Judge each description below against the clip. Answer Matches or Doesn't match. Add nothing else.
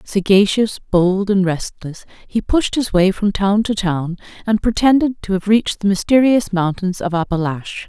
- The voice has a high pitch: Matches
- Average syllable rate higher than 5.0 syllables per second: Doesn't match